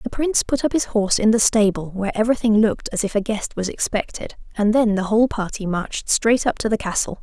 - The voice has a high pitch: Yes, high, 215 Hz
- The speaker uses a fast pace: Yes, fast, 240 wpm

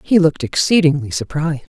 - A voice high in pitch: No, medium, 160 Hz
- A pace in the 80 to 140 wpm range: Yes, slow, 135 wpm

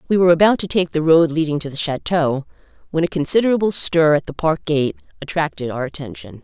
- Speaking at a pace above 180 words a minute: Yes, fast, 205 wpm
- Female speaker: Yes, female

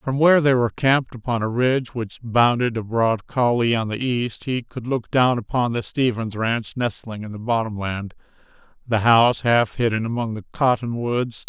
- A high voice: No, low, 120 Hz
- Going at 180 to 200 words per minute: Yes, average, 185 wpm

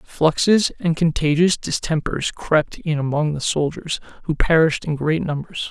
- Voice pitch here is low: No, medium, 155 Hz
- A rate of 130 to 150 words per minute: Yes, average, 145 wpm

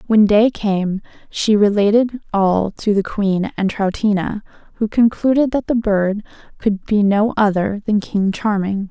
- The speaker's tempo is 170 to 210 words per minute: No, average, 155 wpm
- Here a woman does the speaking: Yes, female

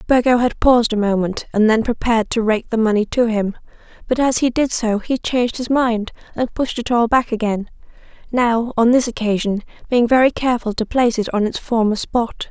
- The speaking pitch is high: Yes, high, 230 Hz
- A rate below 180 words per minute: No, average, 200 wpm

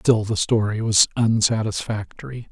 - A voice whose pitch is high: No, low, 110 Hz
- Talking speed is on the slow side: Yes, slow, 120 wpm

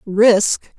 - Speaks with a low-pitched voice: No, high, 210 Hz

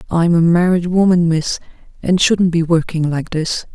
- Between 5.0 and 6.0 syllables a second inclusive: No, 4.6 syllables/s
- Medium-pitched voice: Yes, medium, 170 Hz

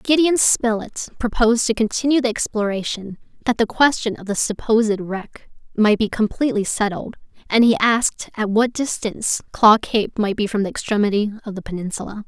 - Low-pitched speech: No, high, 220 Hz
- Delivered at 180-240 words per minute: No, average, 165 wpm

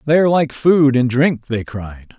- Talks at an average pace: No, fast, 220 wpm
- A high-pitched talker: No, low, 135 Hz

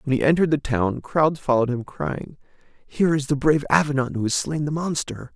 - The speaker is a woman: No, male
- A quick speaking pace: Yes, fast, 215 wpm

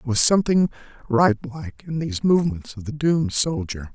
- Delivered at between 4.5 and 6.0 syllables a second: No, 6.2 syllables/s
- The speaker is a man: Yes, male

